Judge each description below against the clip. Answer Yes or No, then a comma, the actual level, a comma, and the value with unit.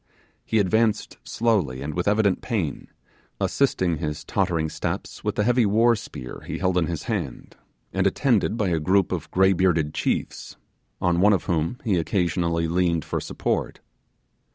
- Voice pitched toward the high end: No, very low, 90 Hz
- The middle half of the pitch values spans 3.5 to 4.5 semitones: Yes, average, 4.0 semitones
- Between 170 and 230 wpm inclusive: No, average, 155 wpm